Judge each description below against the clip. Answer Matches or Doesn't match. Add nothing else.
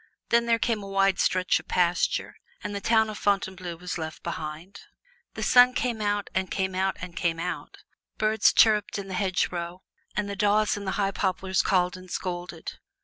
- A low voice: Doesn't match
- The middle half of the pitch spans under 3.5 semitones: Matches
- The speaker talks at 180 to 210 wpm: Matches